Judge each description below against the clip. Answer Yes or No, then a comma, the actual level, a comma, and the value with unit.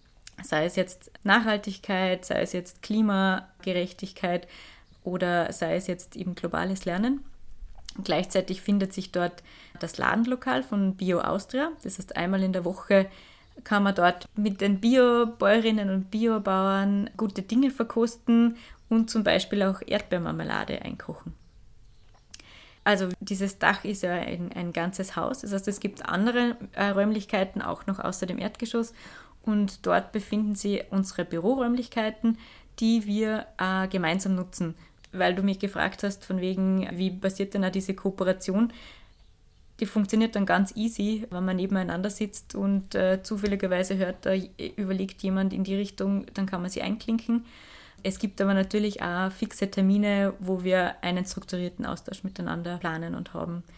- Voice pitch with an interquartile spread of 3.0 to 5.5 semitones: No, narrow, 2.4 semitones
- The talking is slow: No, average, 145 wpm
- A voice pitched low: No, high, 195 Hz